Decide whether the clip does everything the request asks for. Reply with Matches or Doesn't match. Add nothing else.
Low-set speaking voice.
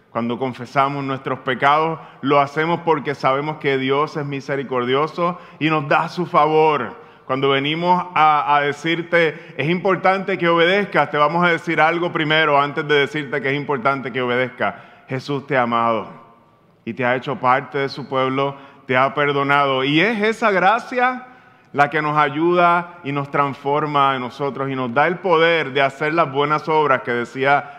Doesn't match